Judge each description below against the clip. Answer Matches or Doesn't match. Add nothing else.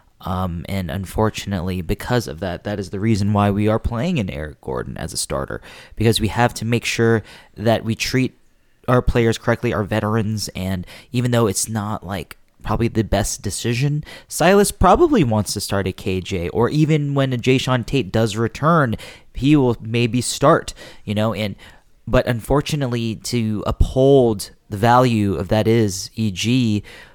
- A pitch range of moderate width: Matches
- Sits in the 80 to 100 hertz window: Doesn't match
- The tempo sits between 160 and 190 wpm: Matches